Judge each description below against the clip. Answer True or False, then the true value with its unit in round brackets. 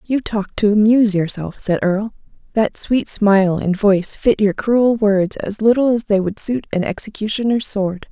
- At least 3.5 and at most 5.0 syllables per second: True (4.8 syllables/s)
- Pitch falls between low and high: False (210 Hz)